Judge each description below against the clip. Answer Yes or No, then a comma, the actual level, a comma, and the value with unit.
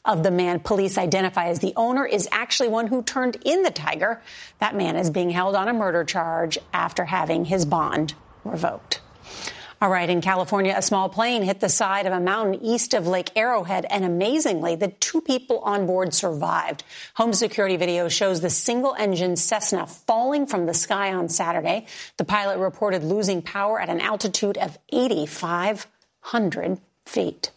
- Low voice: No, high, 195 Hz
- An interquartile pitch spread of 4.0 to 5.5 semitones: No, average, 3.4 semitones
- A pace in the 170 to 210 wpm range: Yes, average, 175 wpm